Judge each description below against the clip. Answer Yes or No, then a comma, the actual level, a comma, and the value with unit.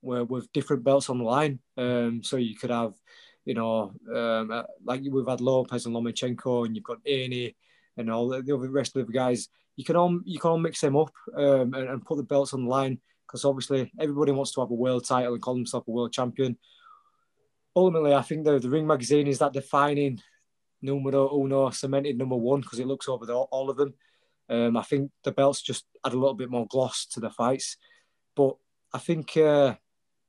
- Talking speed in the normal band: No, fast, 215 wpm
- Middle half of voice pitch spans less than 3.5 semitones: Yes, narrow, 2.5 semitones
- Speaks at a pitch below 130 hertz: No, low, 135 Hz